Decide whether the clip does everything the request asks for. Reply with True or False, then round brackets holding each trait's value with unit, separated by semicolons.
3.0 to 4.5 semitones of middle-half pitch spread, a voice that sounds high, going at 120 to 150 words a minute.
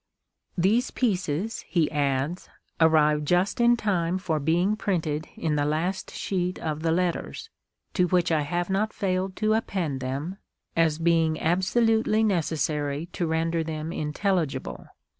False (3.6 semitones; 170 Hz; 140 wpm)